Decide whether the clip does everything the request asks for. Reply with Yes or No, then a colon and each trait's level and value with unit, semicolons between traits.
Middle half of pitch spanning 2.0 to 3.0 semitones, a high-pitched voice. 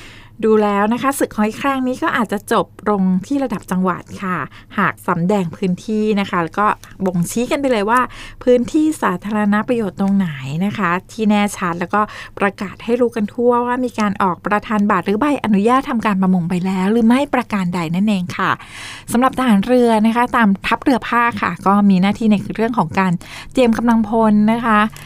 No: average, 3.7 semitones; high, 210 Hz